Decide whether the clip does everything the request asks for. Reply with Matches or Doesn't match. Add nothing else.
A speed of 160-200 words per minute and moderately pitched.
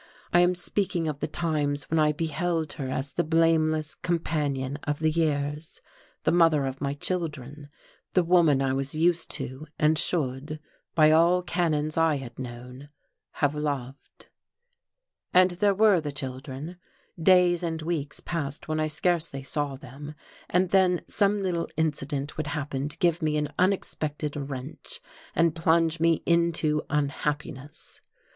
Doesn't match